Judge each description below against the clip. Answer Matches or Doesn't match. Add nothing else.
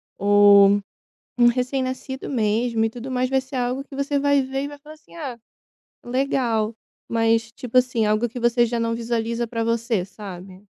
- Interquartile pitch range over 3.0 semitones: Doesn't match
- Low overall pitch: Doesn't match